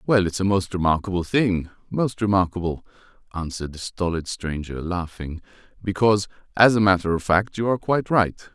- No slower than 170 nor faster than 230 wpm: No, average, 155 wpm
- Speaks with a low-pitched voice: Yes, very low, 95 Hz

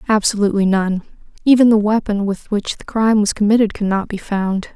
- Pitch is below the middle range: No, high, 210 Hz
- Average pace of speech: Yes, average, 175 wpm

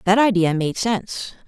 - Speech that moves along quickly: No, average, 165 wpm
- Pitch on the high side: Yes, high, 195 Hz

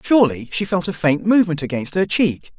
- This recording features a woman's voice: No, male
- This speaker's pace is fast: Yes, fast, 210 wpm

